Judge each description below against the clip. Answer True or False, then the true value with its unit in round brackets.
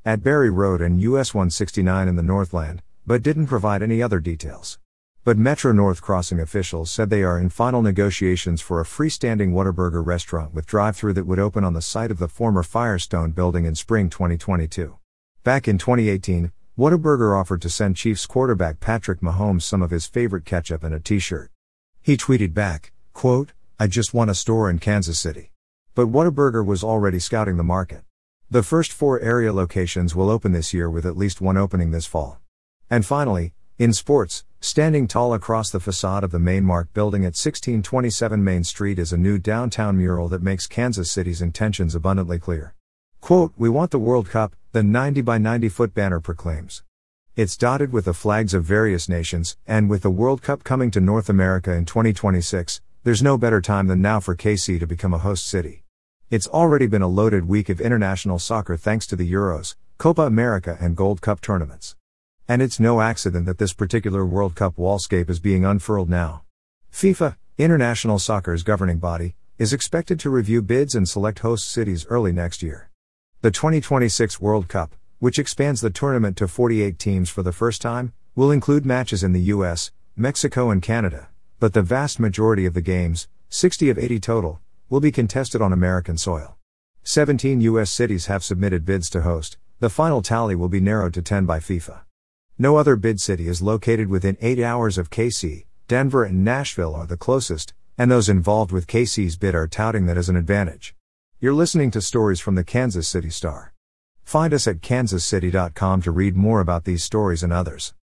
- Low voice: True (100 Hz)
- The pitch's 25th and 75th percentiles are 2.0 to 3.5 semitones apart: False (4.6 semitones)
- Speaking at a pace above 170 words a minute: True (185 wpm)